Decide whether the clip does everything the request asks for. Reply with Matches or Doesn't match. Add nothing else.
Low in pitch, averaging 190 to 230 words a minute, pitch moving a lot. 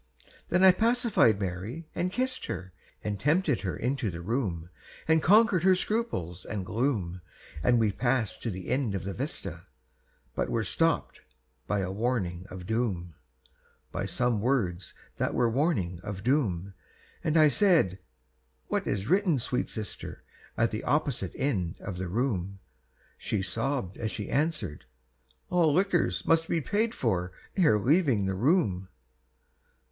Doesn't match